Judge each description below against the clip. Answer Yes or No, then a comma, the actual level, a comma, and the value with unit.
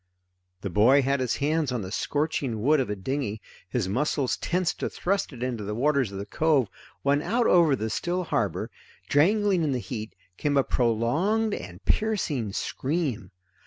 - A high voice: No, low, 135 Hz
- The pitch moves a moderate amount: No, wide, 6.3 semitones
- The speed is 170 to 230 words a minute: Yes, average, 175 wpm